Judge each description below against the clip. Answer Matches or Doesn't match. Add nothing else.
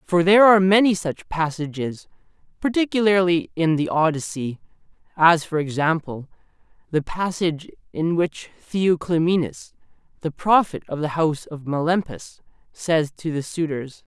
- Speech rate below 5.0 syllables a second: Matches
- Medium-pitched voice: Matches